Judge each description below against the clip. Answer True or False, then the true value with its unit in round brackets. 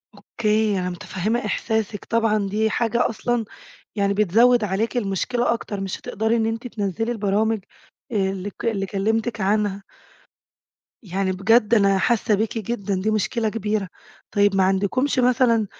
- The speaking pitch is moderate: False (215 Hz)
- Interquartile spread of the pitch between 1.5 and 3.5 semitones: True (2.5 semitones)